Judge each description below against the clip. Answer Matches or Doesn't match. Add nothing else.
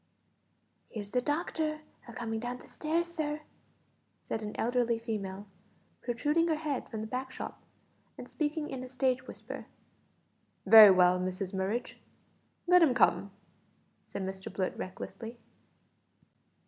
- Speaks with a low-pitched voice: Doesn't match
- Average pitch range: Doesn't match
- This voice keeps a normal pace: Doesn't match